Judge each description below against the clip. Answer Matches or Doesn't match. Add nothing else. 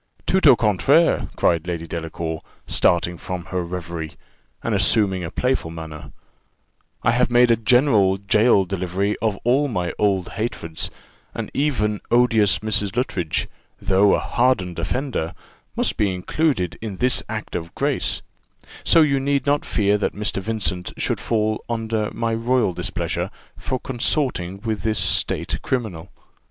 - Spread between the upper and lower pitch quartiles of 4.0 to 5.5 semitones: Matches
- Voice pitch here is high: Doesn't match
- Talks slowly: Doesn't match